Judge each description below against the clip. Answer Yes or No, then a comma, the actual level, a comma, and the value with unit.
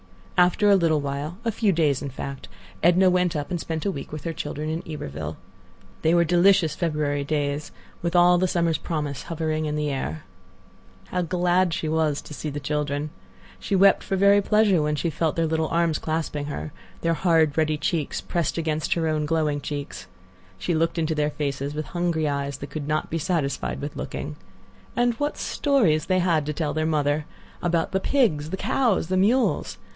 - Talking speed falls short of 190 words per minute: No, average, 195 wpm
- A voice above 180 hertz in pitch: No, medium, 160 Hz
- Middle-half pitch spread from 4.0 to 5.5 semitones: No, average, 3.0 semitones